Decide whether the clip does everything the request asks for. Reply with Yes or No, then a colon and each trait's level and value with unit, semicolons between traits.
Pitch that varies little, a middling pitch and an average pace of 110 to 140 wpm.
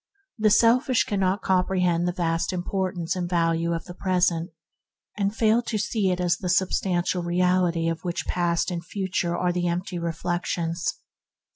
No: narrow, 1.7 semitones; medium, 180 Hz; average, 160 wpm